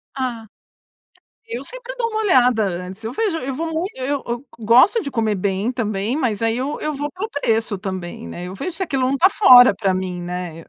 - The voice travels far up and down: Yes, wide, 7.4 semitones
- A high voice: Yes, high, 245 Hz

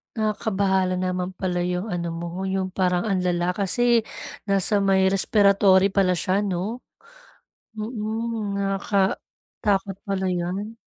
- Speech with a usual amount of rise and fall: No, narrow, 2.0 semitones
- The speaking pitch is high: Yes, high, 195 Hz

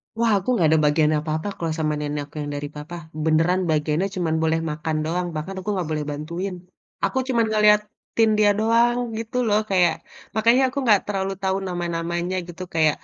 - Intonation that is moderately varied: Yes, average, 4.8 semitones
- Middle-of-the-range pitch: Yes, medium, 175 Hz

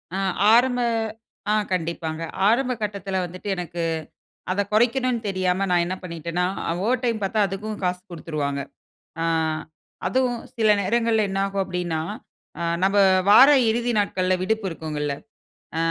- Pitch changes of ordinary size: Yes, average, 4.2 semitones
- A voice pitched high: Yes, high, 195 Hz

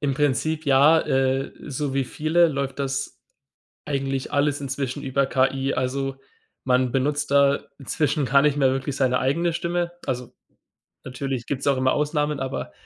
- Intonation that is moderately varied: No, narrow, 1.8 semitones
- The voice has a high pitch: No, low, 135 Hz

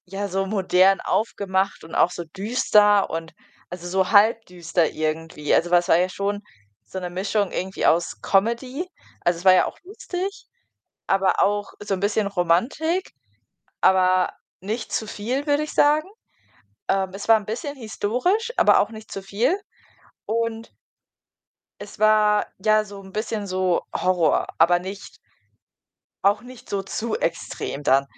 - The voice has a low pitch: No, high, 200 Hz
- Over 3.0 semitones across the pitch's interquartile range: Yes, average, 3.4 semitones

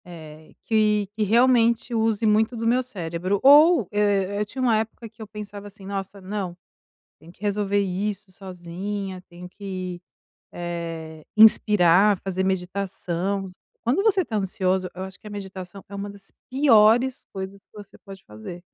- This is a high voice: Yes, high, 200 Hz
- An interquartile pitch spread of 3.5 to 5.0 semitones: No, average, 2.7 semitones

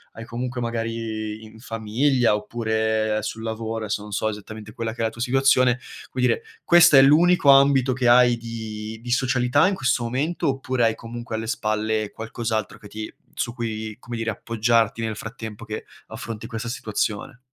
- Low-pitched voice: Yes, low, 115 Hz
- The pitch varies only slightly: Yes, narrow, 2.3 semitones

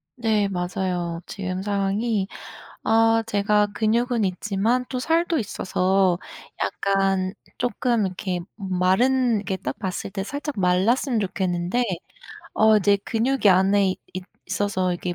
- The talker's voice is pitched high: Yes, high, 200 Hz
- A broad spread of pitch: No, average, 3.4 semitones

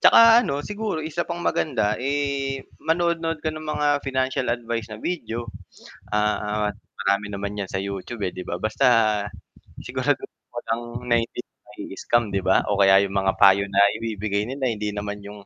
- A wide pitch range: Yes, wide, 5.8 semitones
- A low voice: Yes, low, 115 Hz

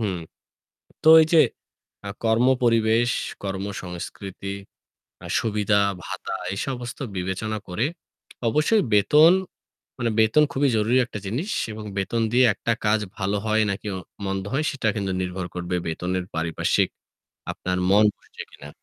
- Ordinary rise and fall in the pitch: Yes, average, 4.0 semitones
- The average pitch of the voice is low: Yes, low, 105 Hz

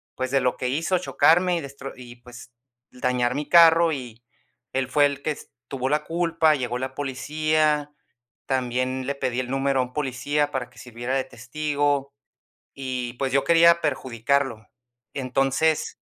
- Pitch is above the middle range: No, low, 135 Hz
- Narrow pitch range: No, average, 3.0 semitones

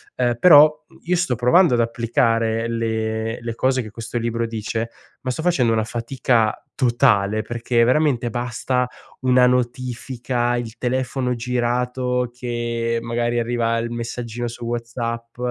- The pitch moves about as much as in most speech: No, narrow, 1.4 semitones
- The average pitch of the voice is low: Yes, low, 120 Hz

